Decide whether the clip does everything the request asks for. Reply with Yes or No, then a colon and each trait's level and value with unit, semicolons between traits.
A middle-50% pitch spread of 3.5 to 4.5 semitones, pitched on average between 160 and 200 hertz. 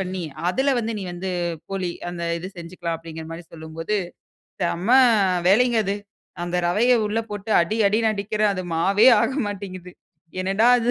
Yes: average, 3.8 semitones; high, 190 Hz